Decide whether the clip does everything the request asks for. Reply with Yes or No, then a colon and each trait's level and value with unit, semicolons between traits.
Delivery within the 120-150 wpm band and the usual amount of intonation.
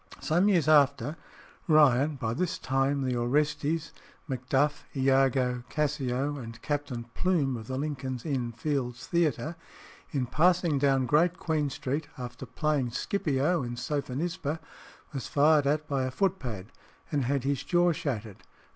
Yes: average, 140 wpm; average, 3.1 semitones